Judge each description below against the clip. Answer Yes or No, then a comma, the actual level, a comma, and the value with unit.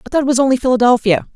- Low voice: No, very high, 250 Hz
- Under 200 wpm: No, fast, 265 wpm